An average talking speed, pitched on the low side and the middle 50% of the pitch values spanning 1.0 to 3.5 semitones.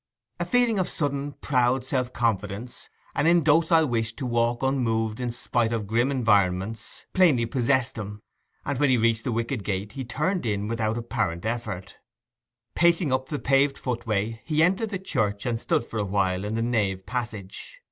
No: average, 175 wpm; low, 120 Hz; average, 4.2 semitones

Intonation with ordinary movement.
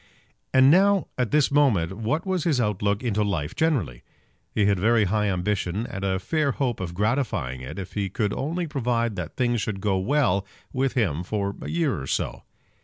No: wide, 5.8 semitones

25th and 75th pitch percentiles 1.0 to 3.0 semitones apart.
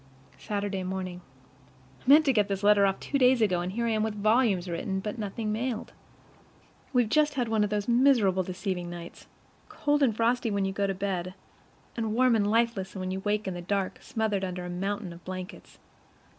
No: average, 3.4 semitones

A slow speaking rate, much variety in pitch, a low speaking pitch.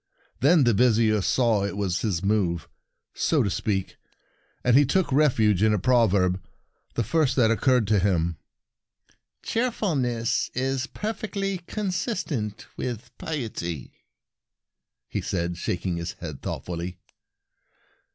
Yes: slow, 125 wpm; wide, 6.1 semitones; low, 115 Hz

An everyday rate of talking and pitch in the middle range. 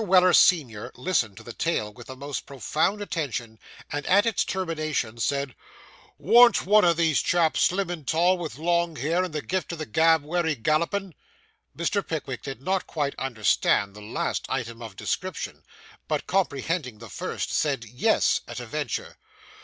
Yes: average, 170 wpm; medium, 155 Hz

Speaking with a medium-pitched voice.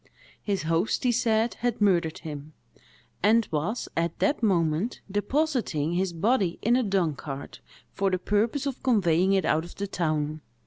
No: high, 195 Hz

